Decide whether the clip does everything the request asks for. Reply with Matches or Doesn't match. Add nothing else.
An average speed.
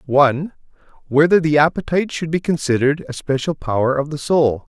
Matches